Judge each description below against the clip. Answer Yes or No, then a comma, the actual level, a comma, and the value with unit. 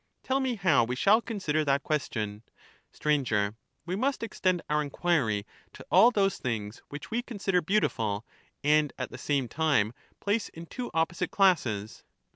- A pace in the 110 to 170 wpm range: Yes, average, 165 wpm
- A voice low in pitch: No, medium, 155 Hz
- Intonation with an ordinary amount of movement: No, wide, 8.1 semitones